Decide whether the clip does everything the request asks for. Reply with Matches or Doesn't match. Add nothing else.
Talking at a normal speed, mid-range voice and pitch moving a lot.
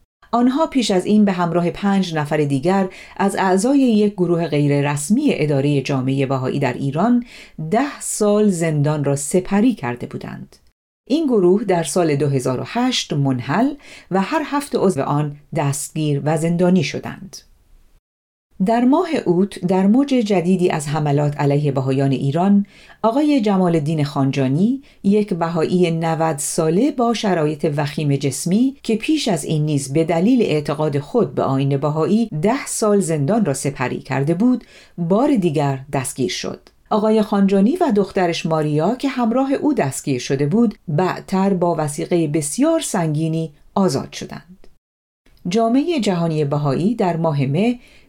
Matches